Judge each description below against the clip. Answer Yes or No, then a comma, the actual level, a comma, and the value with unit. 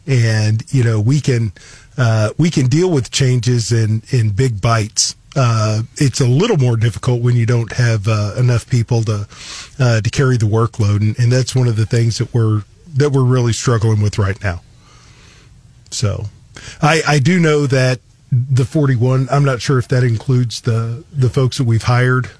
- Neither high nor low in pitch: No, low, 120 Hz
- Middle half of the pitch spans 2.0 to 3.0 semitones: Yes, narrow, 2.6 semitones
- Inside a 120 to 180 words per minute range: No, average, 190 wpm